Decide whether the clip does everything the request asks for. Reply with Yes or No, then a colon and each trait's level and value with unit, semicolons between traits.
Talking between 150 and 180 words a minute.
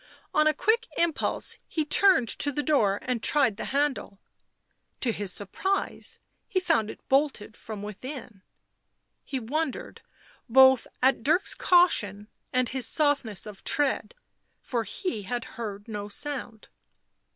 No: slow, 135 wpm